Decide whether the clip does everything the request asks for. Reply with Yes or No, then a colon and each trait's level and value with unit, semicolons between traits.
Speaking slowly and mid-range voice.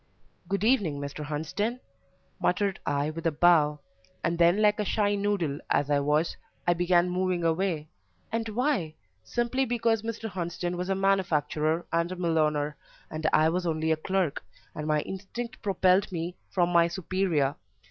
No: average, 160 wpm; medium, 175 Hz